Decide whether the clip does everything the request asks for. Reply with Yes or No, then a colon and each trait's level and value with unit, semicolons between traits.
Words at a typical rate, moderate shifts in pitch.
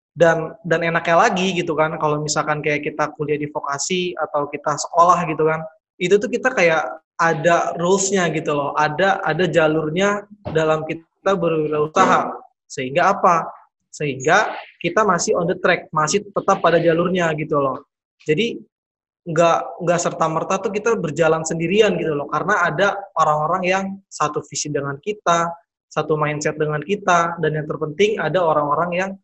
No: fast, 155 wpm; average, 3.3 semitones